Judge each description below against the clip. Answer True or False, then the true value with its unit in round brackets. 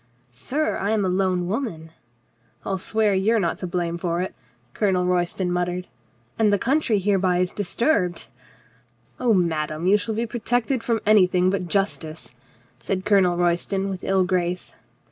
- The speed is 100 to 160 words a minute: False (185 wpm)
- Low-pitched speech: False (185 Hz)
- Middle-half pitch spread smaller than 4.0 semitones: True (3.0 semitones)